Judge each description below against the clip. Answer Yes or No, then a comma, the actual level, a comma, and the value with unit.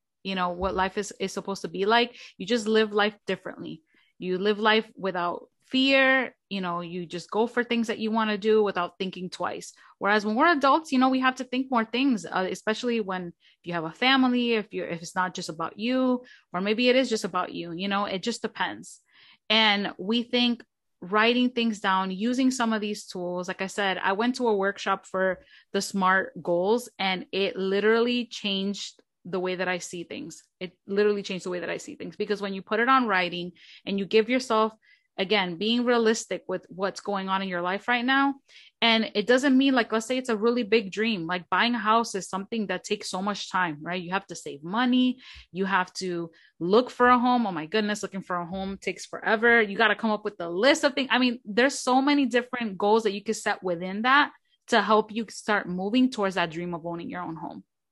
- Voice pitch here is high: Yes, high, 210 Hz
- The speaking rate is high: Yes, fast, 230 wpm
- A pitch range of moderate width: Yes, average, 4.2 semitones